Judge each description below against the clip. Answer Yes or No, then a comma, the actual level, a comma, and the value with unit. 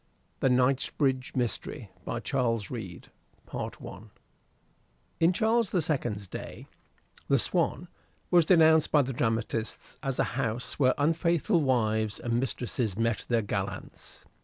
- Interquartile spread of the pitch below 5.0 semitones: No, wide, 5.4 semitones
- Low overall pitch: Yes, low, 125 Hz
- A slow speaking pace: Yes, slow, 125 wpm